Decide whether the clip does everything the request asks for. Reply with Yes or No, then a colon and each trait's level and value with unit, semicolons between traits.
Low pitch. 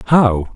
Yes: low, 120 Hz